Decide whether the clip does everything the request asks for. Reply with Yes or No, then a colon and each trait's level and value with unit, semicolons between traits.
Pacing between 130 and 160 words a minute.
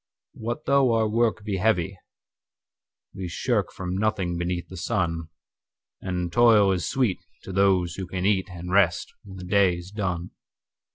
Yes: average, 140 wpm